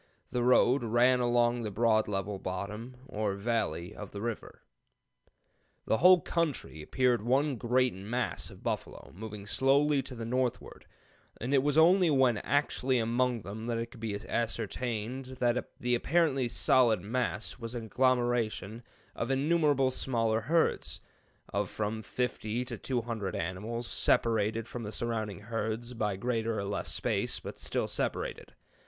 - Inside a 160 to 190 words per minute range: No, average, 150 wpm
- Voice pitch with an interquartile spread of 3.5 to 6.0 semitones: No, average, 2.9 semitones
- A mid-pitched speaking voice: No, low, 120 Hz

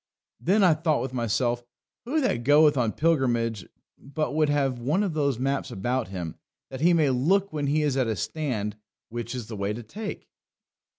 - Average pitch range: Yes, average, 4.8 semitones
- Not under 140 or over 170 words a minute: No, average, 190 wpm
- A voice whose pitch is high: No, low, 135 Hz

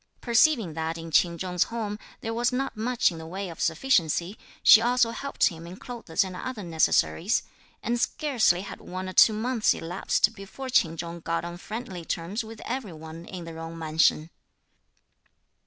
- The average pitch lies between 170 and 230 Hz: Yes, medium, 185 Hz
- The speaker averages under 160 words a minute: No, average, 175 wpm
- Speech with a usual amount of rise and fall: No, wide, 5.8 semitones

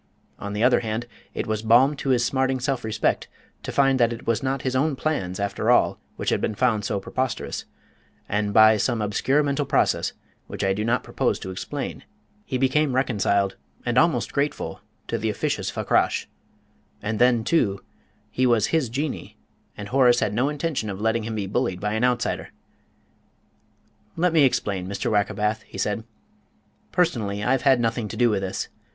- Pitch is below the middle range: Yes, low, 115 Hz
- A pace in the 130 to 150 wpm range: No, average, 180 wpm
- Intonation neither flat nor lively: Yes, average, 4.1 semitones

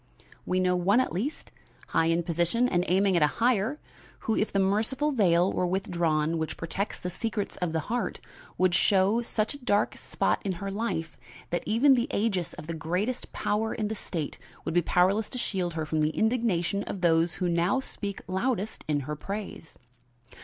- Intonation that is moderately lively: Yes, average, 4.4 semitones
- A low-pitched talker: No, high, 190 Hz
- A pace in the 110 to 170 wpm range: No, average, 190 wpm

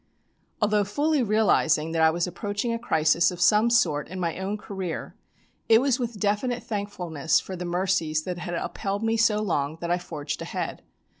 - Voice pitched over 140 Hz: Yes, high, 190 Hz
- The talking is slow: No, average, 180 wpm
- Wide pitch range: No, average, 4.3 semitones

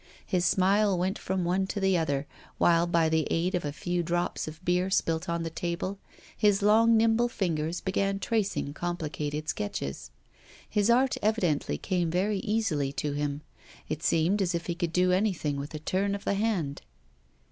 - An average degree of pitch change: Yes, average, 3.7 semitones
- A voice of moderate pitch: Yes, medium, 175 Hz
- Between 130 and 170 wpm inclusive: No, average, 180 wpm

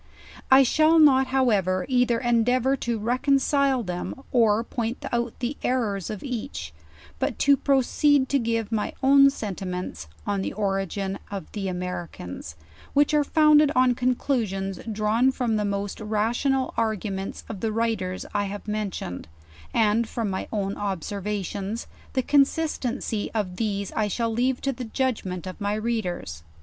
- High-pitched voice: Yes, high, 225 Hz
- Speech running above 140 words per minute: Yes, average, 150 wpm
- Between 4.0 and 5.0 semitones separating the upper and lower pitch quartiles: Yes, average, 4.5 semitones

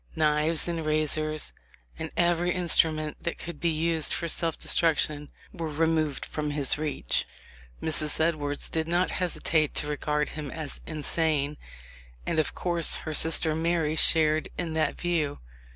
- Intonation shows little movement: Yes, narrow, 1.6 semitones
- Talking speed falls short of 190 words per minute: Yes, average, 145 wpm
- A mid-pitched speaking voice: Yes, medium, 155 Hz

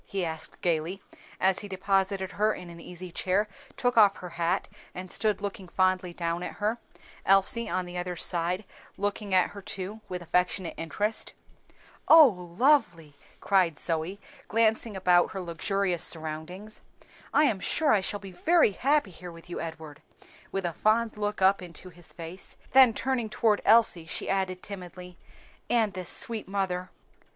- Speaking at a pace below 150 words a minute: No, average, 165 wpm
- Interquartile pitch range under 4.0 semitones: Yes, average, 3.0 semitones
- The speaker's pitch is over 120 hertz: Yes, high, 190 Hz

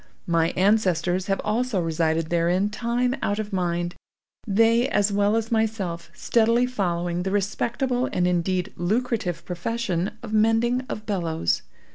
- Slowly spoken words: Yes, slow, 130 wpm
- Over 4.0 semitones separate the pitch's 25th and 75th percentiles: Yes, average, 4.5 semitones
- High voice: Yes, high, 200 Hz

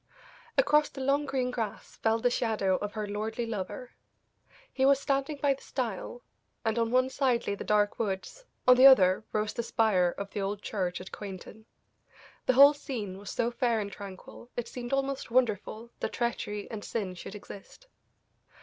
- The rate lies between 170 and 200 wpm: Yes, average, 180 wpm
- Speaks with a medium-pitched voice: No, high, 225 Hz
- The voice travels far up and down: No, average, 4.0 semitones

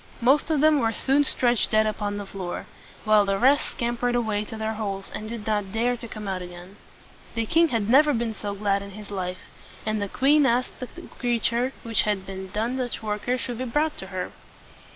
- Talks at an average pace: No, fast, 215 wpm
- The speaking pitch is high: Yes, high, 220 Hz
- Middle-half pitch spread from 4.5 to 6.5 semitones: No, average, 3.4 semitones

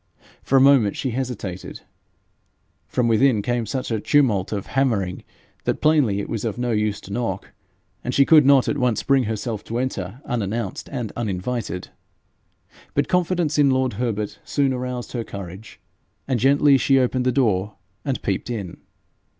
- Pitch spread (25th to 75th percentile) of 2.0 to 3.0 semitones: No, average, 4.2 semitones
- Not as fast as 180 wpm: Yes, average, 165 wpm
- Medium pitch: No, low, 120 Hz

